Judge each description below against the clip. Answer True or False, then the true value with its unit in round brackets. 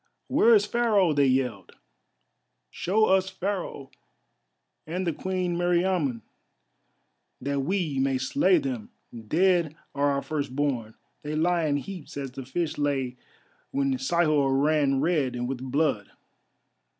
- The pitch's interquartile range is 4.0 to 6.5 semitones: True (5.0 semitones)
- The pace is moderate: False (125 wpm)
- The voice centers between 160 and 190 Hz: False (150 Hz)